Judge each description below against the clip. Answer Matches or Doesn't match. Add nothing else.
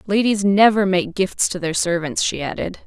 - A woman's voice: Matches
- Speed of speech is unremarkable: Matches